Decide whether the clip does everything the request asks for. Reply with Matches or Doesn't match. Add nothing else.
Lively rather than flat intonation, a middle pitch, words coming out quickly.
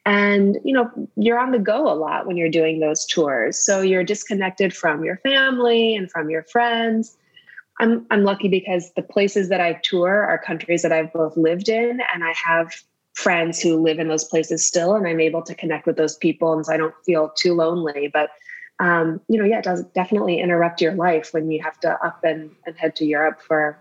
Doesn't match